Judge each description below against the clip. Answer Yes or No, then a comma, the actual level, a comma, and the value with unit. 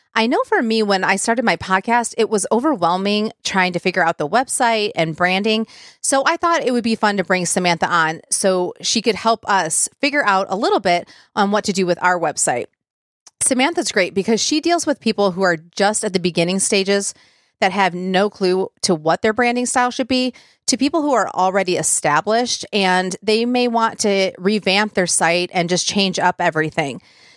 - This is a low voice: No, high, 200 Hz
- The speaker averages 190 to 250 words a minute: Yes, average, 200 wpm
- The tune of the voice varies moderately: Yes, average, 3.9 semitones